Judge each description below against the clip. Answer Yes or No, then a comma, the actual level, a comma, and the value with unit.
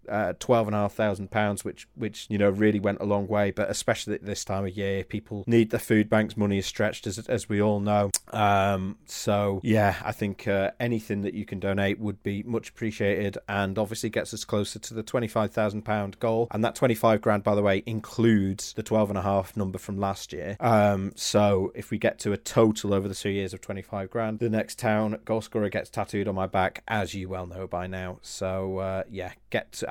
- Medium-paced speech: No, fast, 215 wpm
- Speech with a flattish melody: Yes, narrow, 1.8 semitones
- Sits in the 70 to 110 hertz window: Yes, low, 105 Hz